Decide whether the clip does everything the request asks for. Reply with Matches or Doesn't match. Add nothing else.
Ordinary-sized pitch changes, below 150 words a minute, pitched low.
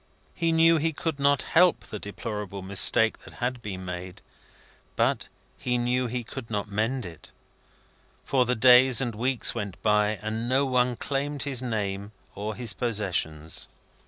Doesn't match